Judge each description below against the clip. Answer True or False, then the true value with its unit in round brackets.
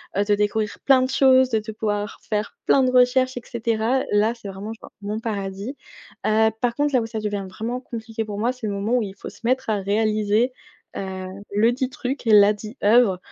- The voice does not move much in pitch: False (3.2 semitones)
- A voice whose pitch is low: False (220 Hz)